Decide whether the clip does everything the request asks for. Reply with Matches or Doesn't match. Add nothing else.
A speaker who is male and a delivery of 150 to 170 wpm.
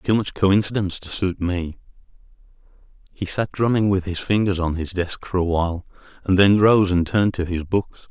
Doesn't match